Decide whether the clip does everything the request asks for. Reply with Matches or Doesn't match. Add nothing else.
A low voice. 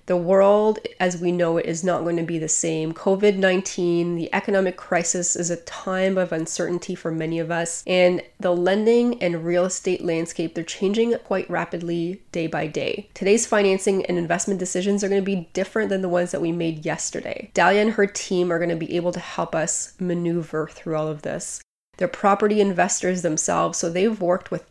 Doesn't match